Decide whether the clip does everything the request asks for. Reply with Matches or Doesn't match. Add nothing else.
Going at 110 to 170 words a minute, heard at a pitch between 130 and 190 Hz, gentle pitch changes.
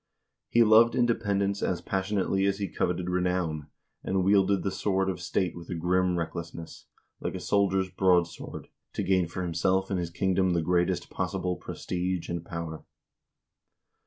Doesn't match